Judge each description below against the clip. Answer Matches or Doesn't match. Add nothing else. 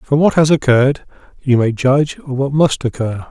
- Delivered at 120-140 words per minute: Doesn't match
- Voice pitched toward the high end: Doesn't match